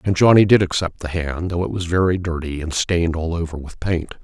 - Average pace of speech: No, fast, 240 wpm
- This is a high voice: No, very low, 85 Hz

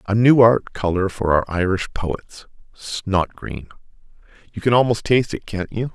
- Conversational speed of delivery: Yes, average, 160 wpm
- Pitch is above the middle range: No, low, 100 Hz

